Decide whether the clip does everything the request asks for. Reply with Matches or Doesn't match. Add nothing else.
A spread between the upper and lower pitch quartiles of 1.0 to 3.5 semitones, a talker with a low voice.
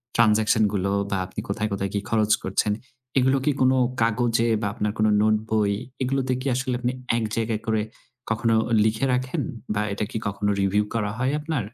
Matches